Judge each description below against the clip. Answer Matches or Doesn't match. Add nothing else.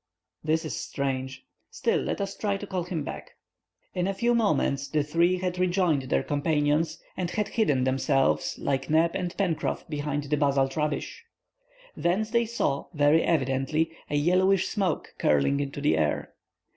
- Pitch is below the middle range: Doesn't match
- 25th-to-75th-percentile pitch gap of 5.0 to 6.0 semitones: Doesn't match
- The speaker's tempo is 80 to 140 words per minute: Doesn't match